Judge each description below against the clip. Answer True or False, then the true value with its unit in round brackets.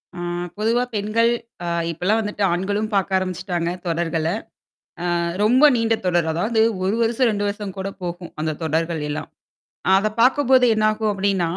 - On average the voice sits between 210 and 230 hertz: False (200 Hz)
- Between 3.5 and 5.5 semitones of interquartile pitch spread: True (4.1 semitones)